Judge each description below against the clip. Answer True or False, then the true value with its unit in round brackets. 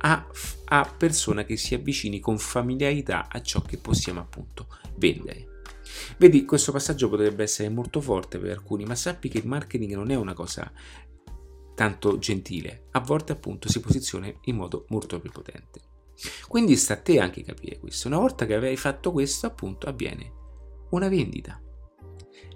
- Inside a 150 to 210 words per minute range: True (160 wpm)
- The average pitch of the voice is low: True (105 Hz)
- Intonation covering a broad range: True (8.1 semitones)